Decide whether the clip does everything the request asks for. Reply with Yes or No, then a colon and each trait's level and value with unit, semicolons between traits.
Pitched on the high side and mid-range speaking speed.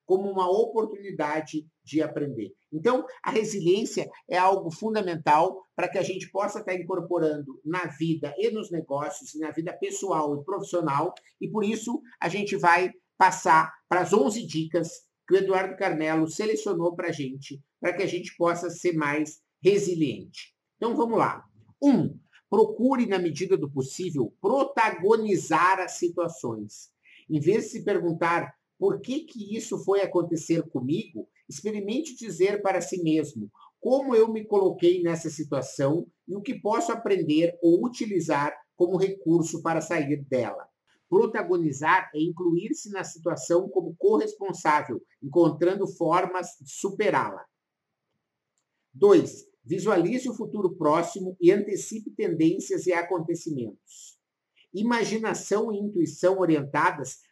No: medium, 180 Hz; average, 135 wpm